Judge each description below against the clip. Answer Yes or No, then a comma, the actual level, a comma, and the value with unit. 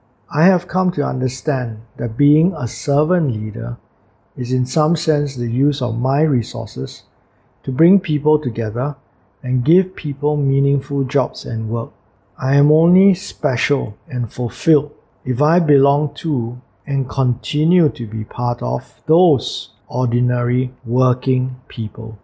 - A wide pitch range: No, average, 4.0 semitones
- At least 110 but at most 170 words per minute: Yes, slow, 135 wpm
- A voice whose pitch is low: Yes, low, 130 Hz